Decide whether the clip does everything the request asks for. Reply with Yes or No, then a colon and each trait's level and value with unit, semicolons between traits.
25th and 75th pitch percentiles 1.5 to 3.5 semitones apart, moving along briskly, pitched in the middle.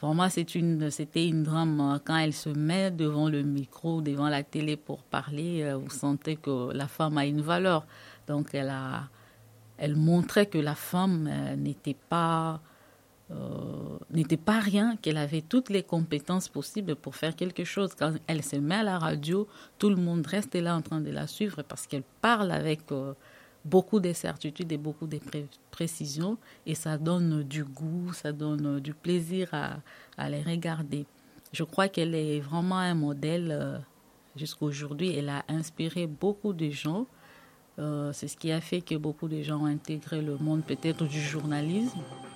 No: average, 2.7 semitones; average, 180 wpm; medium, 155 Hz